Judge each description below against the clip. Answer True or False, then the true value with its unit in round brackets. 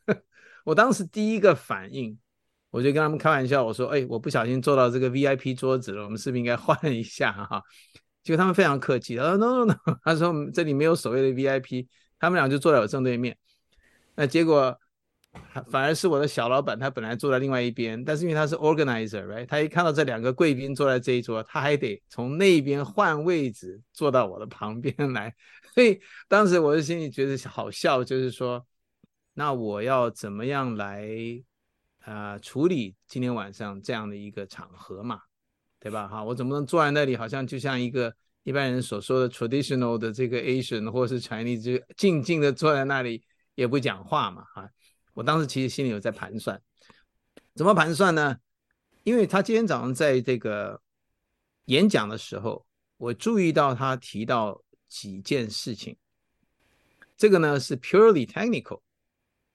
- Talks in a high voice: False (130 Hz)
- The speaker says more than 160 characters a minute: True (320 characters per minute)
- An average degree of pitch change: True (4.5 semitones)